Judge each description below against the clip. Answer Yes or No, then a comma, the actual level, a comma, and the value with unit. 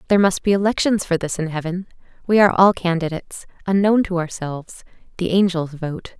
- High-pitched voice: No, medium, 180 Hz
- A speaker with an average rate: Yes, average, 175 wpm